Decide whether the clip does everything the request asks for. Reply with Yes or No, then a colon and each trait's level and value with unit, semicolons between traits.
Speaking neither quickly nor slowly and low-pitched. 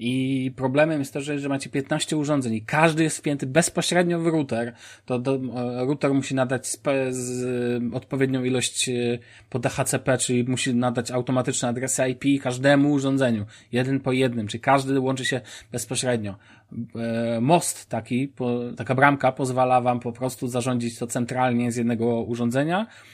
Yes: average, 135 wpm; low, 130 Hz